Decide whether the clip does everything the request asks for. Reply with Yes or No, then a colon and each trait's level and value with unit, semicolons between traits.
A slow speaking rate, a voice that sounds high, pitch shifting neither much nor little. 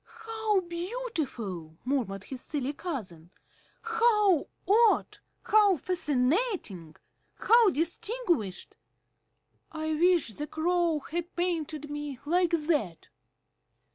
No: slow, 90 wpm; very high, 325 Hz; wide, 6.0 semitones